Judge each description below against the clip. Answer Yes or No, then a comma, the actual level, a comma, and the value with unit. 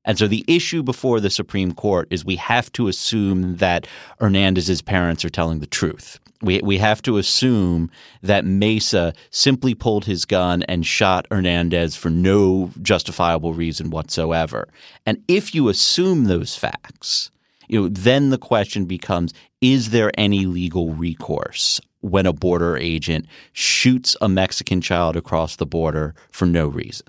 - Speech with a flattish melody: No, average, 4.2 semitones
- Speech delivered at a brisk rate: No, average, 155 wpm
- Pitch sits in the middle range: No, very low, 95 Hz